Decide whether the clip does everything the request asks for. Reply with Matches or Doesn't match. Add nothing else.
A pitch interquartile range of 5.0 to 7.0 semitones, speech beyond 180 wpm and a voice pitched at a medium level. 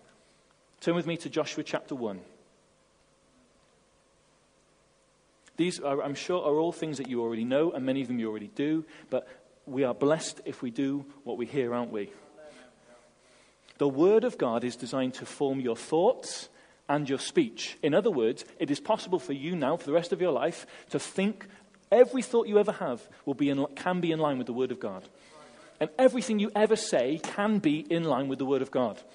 Matches